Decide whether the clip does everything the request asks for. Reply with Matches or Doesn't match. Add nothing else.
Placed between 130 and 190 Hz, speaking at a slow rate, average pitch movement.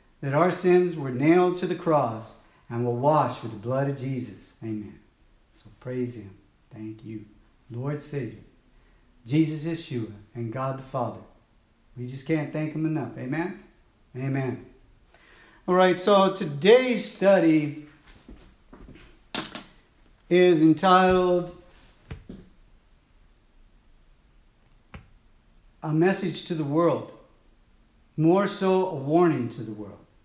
Doesn't match